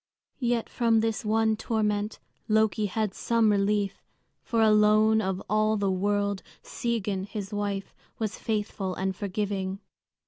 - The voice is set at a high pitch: Yes, high, 210 Hz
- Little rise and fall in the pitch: Yes, narrow, 1.7 semitones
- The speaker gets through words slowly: Yes, slow, 130 wpm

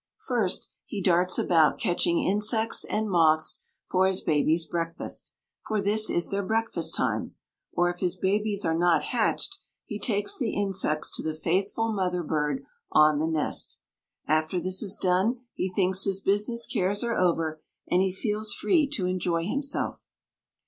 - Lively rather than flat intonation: No, average, 3.8 semitones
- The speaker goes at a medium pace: Yes, average, 160 wpm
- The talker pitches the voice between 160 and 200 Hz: Yes, medium, 185 Hz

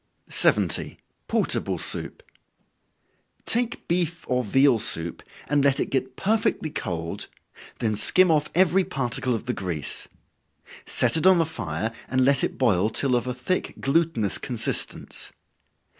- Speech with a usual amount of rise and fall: No, wide, 6.6 semitones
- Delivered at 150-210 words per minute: No, average, 140 wpm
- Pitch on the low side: Yes, low, 130 Hz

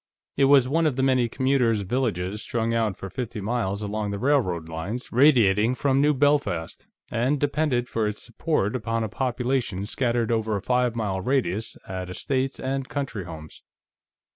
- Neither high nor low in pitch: No, low, 120 Hz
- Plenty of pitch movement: No, average, 4.5 semitones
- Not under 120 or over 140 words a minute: No, average, 165 wpm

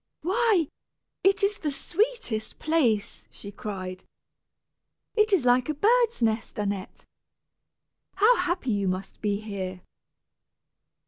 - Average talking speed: No, slow, 115 wpm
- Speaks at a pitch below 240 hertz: No, very high, 260 Hz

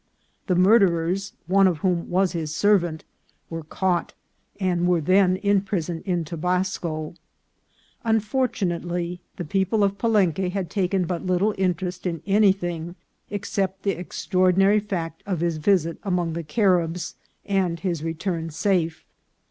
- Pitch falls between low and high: Yes, medium, 180 Hz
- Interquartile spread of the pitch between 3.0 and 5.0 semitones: No, narrow, 2.6 semitones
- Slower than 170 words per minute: Yes, average, 140 wpm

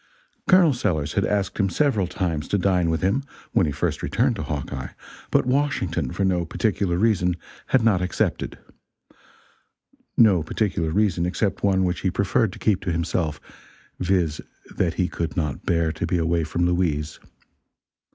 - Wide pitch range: No, average, 3.5 semitones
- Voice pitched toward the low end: Yes, very low, 90 Hz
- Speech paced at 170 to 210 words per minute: No, average, 160 wpm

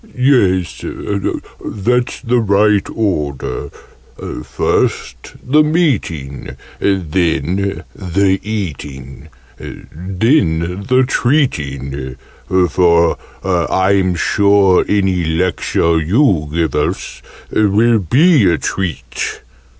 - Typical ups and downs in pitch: Yes, average, 4.7 semitones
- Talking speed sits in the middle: No, slow, 80 wpm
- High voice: No, very low, 95 Hz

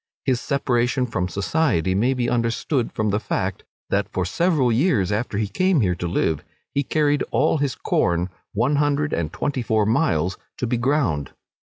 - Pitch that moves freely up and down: Yes, wide, 6.7 semitones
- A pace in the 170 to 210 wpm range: Yes, average, 175 wpm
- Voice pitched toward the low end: Yes, low, 120 Hz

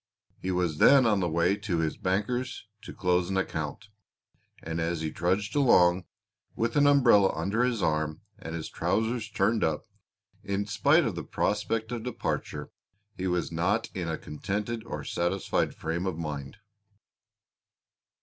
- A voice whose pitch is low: Yes, very low, 95 Hz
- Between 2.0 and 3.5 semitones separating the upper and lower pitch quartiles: No, average, 4.9 semitones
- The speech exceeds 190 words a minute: No, average, 155 wpm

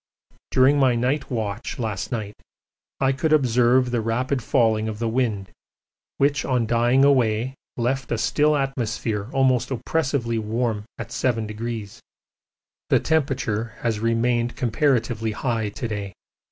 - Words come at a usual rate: No, slow, 130 wpm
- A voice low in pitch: Yes, low, 120 Hz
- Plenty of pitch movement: No, average, 2.8 semitones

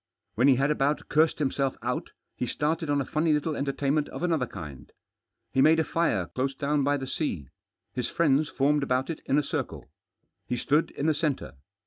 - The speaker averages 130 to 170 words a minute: No, average, 200 wpm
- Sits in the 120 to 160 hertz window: Yes, medium, 140 Hz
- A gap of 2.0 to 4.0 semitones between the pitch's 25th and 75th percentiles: Yes, narrow, 2.5 semitones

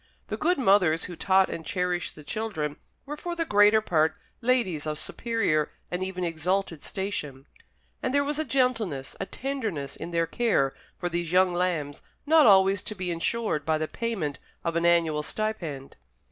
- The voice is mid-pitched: Yes, medium, 180 Hz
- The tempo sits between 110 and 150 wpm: No, average, 175 wpm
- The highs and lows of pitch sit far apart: Yes, wide, 5.8 semitones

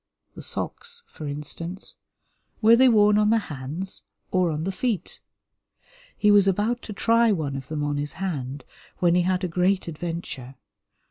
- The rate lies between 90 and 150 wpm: No, average, 165 wpm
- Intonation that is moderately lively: No, wide, 5.7 semitones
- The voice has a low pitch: No, medium, 180 Hz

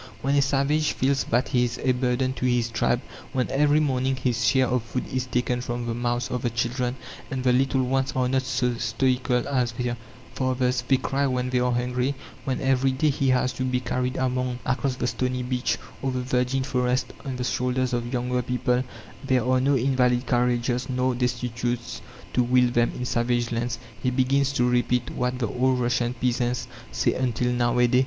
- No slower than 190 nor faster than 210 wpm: Yes, average, 200 wpm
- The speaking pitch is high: No, low, 125 Hz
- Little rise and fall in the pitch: Yes, narrow, 1.1 semitones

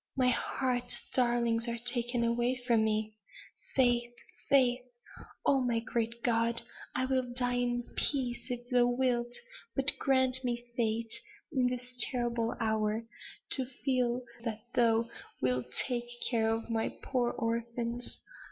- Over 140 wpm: No, slow, 135 wpm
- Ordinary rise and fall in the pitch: No, narrow, 1.3 semitones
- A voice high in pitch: Yes, high, 240 Hz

